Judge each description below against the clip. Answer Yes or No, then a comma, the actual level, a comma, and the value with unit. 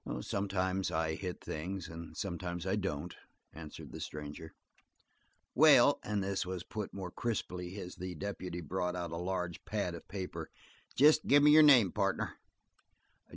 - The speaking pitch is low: Yes, very low, 90 Hz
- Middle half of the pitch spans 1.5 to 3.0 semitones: Yes, narrow, 2.6 semitones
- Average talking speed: Yes, average, 150 wpm